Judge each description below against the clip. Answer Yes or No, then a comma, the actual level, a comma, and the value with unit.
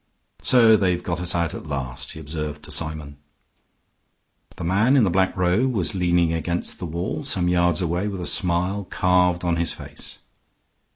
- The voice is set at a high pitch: No, very low, 90 Hz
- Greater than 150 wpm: Yes, average, 175 wpm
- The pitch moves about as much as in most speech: No, narrow, 2.2 semitones